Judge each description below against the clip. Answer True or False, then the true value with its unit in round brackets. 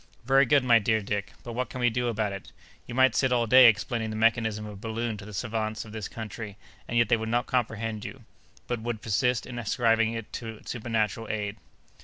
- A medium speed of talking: False (225 wpm)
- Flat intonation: True (1.9 semitones)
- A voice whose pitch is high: False (115 Hz)